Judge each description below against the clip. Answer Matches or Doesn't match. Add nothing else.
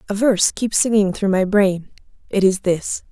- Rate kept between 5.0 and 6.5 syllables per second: Doesn't match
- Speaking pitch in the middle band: Doesn't match